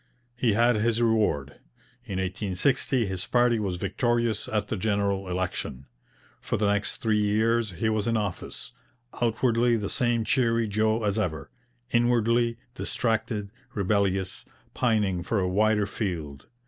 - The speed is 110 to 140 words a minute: Yes, slow, 135 wpm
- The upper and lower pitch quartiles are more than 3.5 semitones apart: No, average, 3.0 semitones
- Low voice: Yes, low, 110 Hz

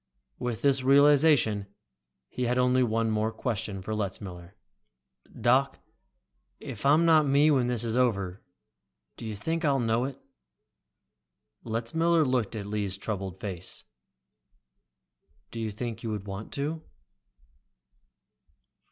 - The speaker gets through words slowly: Yes, slow, 125 wpm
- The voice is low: Yes, low, 115 Hz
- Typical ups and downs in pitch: Yes, average, 4.7 semitones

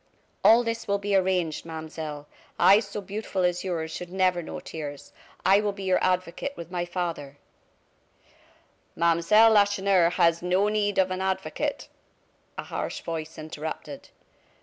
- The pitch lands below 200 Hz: Yes, medium, 185 Hz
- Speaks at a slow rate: No, average, 150 wpm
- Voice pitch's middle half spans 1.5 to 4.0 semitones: Yes, average, 3.3 semitones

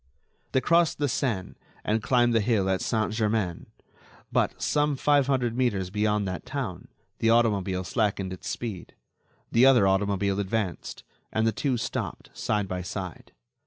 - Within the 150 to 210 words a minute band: Yes, average, 155 wpm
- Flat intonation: No, average, 3.9 semitones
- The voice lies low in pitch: Yes, low, 110 Hz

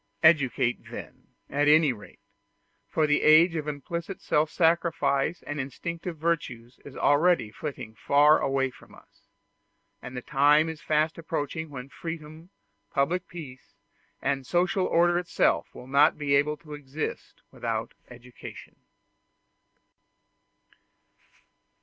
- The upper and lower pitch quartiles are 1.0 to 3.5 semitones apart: Yes, average, 3.0 semitones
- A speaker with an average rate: No, slow, 120 wpm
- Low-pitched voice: No, medium, 150 Hz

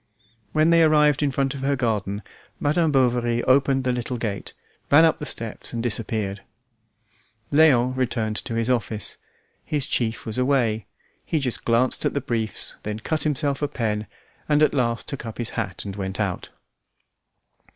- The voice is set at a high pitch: No, low, 125 Hz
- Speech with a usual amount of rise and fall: Yes, average, 4.1 semitones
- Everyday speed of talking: Yes, average, 170 wpm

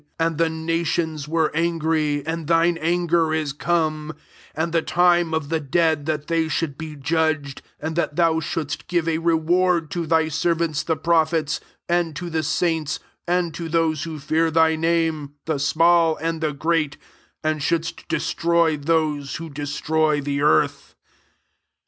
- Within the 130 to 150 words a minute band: No, average, 170 wpm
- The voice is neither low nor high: Yes, medium, 160 Hz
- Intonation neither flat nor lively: No, narrow, 1.5 semitones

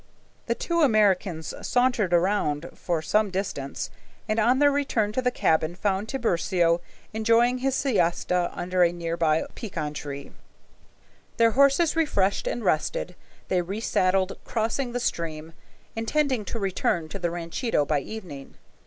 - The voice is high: Yes, high, 195 Hz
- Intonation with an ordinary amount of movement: No, wide, 5.8 semitones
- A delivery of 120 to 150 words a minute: Yes, average, 140 wpm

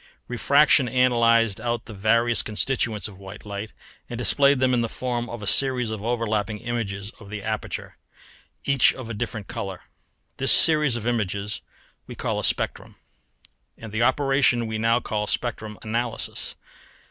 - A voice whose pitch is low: Yes, low, 115 Hz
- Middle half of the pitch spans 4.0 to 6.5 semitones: No, narrow, 2.4 semitones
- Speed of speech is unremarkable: Yes, average, 160 wpm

